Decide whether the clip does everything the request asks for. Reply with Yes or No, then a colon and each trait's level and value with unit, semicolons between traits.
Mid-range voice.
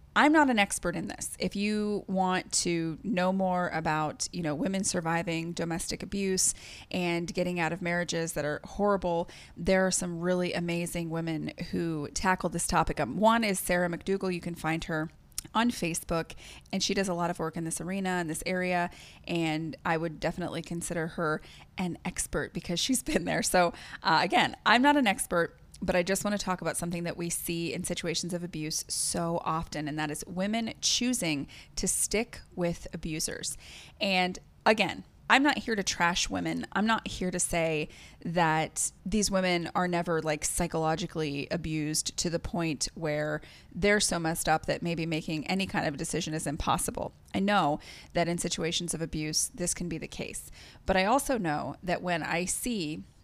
Yes: medium, 175 Hz